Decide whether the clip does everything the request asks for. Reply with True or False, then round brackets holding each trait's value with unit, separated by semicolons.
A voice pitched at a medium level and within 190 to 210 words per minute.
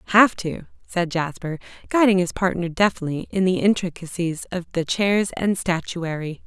False (180 Hz; 150 wpm)